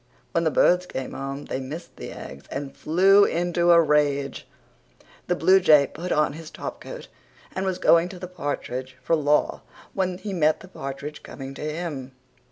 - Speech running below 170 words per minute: No, average, 175 wpm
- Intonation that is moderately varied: Yes, average, 4.2 semitones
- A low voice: No, medium, 155 Hz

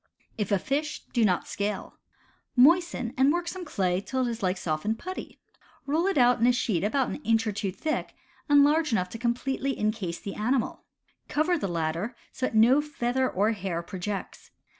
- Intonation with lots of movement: Yes, wide, 6.0 semitones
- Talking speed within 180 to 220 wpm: Yes, average, 190 wpm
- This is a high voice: Yes, high, 235 Hz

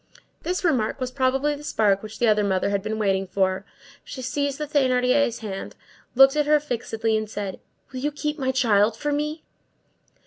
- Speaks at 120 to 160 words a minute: No, average, 185 wpm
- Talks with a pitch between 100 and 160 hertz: No, very high, 250 Hz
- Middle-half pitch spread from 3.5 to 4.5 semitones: No, average, 5.3 semitones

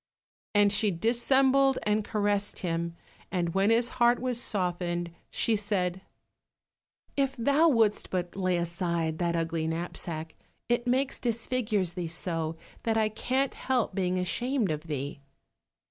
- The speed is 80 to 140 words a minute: Yes, slow, 135 wpm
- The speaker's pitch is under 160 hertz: No, high, 200 Hz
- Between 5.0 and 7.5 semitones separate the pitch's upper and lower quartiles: Yes, wide, 5.6 semitones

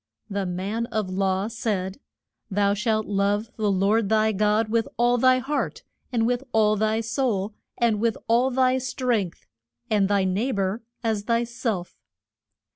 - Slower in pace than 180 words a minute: Yes, average, 155 wpm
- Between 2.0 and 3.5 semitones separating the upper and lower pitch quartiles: Yes, average, 2.8 semitones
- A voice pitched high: Yes, high, 215 Hz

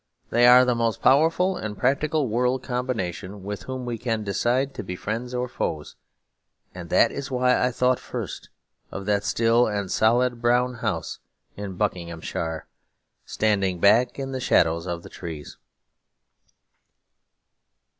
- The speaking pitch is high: No, low, 115 Hz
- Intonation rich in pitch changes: No, average, 4.3 semitones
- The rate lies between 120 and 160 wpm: Yes, average, 145 wpm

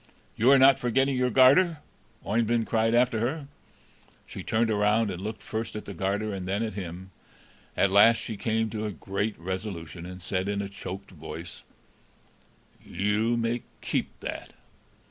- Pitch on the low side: Yes, low, 105 Hz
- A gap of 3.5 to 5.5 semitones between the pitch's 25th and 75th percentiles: No, average, 3.1 semitones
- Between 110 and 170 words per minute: Yes, average, 165 wpm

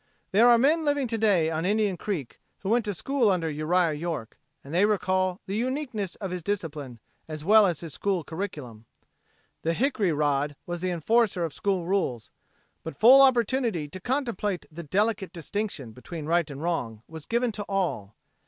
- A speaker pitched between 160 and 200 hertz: Yes, medium, 185 Hz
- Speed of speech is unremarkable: Yes, average, 180 wpm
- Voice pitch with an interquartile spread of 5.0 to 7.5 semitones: Yes, wide, 5.5 semitones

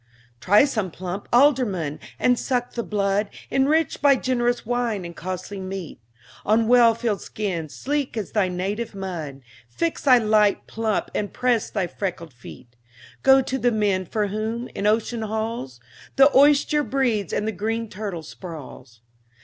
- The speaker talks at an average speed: Yes, average, 155 wpm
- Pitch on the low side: No, high, 215 Hz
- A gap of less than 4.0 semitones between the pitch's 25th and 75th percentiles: No, average, 4.6 semitones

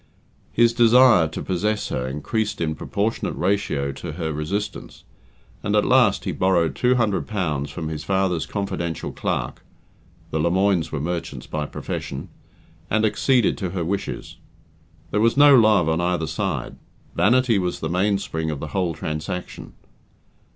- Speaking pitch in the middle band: No, very low, 90 Hz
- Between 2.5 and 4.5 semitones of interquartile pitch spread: No, average, 4.9 semitones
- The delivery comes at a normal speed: Yes, average, 150 wpm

